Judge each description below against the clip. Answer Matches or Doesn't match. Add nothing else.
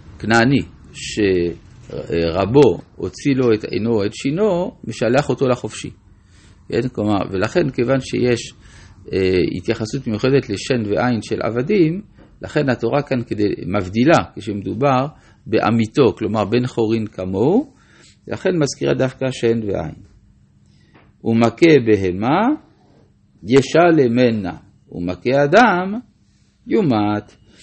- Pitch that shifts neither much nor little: Matches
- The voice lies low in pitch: Matches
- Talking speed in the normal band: Doesn't match